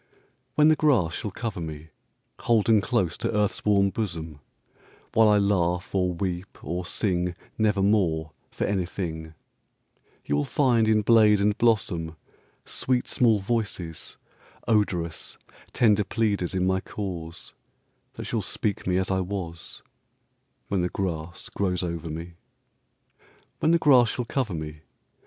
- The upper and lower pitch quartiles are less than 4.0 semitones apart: No, average, 4.3 semitones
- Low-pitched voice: Yes, very low, 95 Hz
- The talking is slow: Yes, slow, 115 wpm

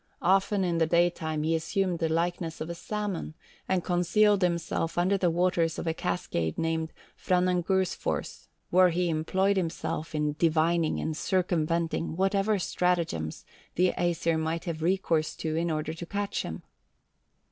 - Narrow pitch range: Yes, narrow, 2.1 semitones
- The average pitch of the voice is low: No, medium, 170 Hz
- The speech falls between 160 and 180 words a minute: No, average, 145 wpm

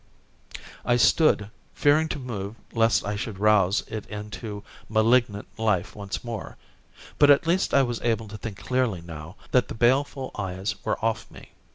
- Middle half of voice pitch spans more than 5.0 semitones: No, average, 3.6 semitones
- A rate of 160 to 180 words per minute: Yes, average, 165 wpm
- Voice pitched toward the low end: Yes, low, 110 Hz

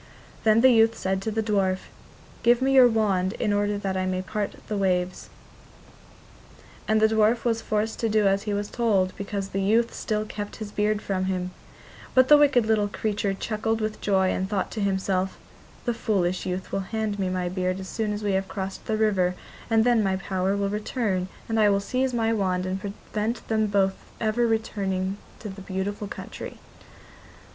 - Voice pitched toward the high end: Yes, high, 205 Hz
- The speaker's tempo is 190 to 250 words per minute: Yes, average, 195 wpm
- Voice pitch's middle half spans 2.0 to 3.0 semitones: Yes, narrow, 2.5 semitones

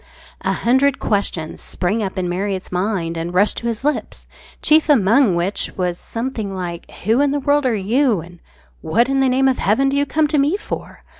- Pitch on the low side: No, high, 225 Hz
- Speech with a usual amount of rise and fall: No, wide, 6.7 semitones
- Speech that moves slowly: No, fast, 205 wpm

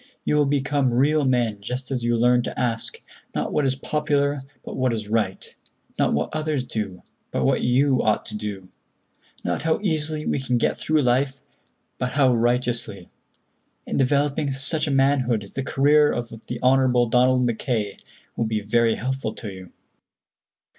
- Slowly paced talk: No, average, 165 wpm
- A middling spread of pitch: Yes, average, 3.6 semitones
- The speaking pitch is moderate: No, low, 125 Hz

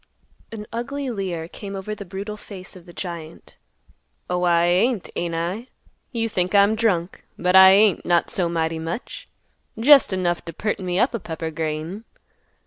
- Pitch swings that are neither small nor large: Yes, average, 3.7 semitones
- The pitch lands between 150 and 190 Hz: Yes, medium, 185 Hz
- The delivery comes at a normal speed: Yes, average, 170 wpm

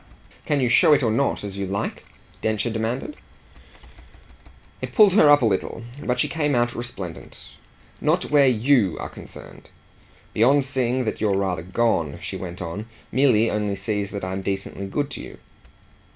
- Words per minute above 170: No, average, 165 wpm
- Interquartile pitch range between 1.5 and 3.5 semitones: No, average, 4.9 semitones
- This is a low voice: Yes, low, 110 Hz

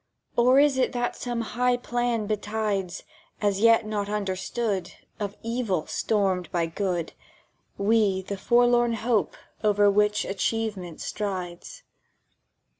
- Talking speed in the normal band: No, slow, 115 wpm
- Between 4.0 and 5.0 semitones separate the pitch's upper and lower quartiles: No, average, 3.4 semitones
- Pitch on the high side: Yes, high, 210 Hz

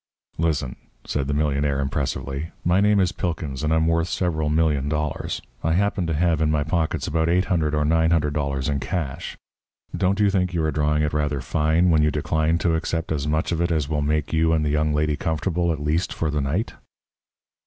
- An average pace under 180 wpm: No, fast, 205 wpm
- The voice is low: Yes, very low, 80 Hz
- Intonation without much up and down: Yes, narrow, 2.0 semitones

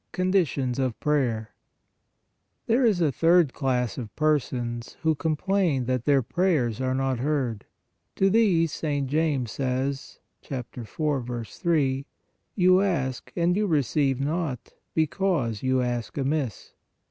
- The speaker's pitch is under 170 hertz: Yes, medium, 140 Hz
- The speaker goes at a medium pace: No, slow, 125 wpm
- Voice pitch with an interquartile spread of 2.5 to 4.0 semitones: No, average, 4.6 semitones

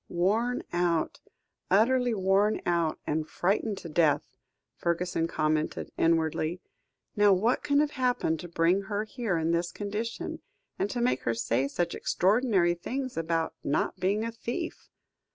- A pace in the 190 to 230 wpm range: No, average, 145 wpm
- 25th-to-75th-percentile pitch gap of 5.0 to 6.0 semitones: Yes, average, 5.3 semitones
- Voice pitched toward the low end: No, medium, 185 Hz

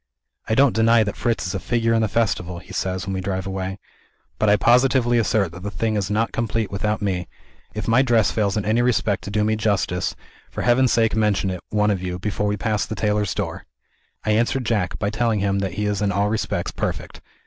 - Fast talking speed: Yes, fast, 230 wpm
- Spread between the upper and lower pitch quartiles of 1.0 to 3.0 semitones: Yes, average, 2.7 semitones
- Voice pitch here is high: No, low, 105 Hz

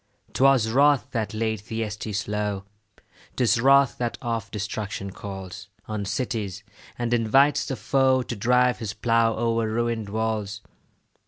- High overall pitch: No, low, 110 Hz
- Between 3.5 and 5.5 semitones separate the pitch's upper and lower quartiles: No, average, 2.7 semitones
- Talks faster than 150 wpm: No, slow, 135 wpm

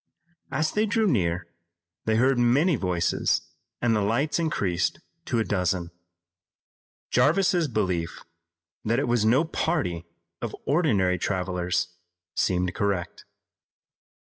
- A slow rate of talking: Yes, slow, 115 wpm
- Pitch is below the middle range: Yes, low, 110 Hz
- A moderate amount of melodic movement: No, wide, 7.9 semitones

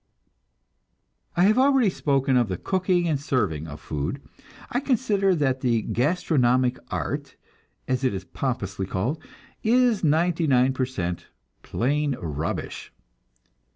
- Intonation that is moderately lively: No, wide, 7.1 semitones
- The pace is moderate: No, slow, 125 wpm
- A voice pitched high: No, low, 135 Hz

